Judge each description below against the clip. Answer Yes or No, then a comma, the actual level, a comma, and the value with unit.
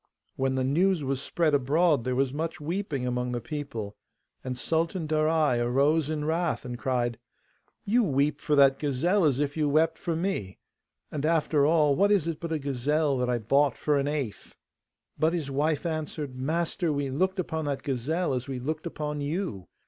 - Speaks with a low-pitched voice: No, medium, 150 Hz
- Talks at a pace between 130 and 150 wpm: No, average, 185 wpm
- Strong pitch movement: No, average, 3.4 semitones